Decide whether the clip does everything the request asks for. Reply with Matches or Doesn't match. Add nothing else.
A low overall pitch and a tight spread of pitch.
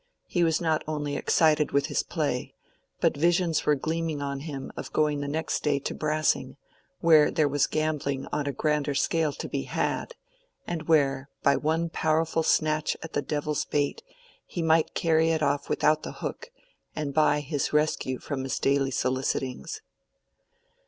Doesn't match